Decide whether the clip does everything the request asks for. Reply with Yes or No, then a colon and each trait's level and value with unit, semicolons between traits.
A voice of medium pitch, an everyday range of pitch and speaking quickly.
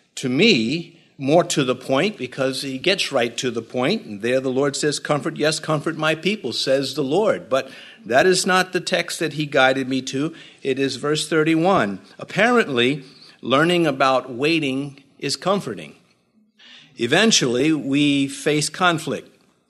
No: medium, 150 Hz; average, 4.1 semitones; average, 155 wpm